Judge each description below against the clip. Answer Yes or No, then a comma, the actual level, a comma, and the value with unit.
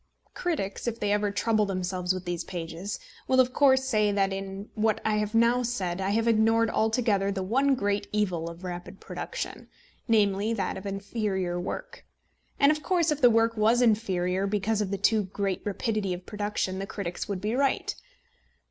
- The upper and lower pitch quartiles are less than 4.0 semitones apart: Yes, average, 3.0 semitones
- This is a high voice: Yes, high, 205 Hz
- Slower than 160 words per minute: No, average, 185 wpm